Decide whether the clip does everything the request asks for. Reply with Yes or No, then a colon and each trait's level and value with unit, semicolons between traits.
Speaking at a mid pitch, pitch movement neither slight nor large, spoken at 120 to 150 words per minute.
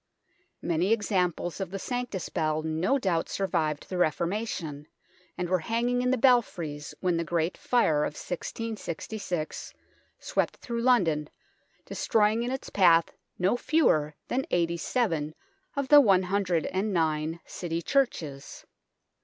No: medium, 180 Hz; wide, 5.9 semitones; slow, 135 wpm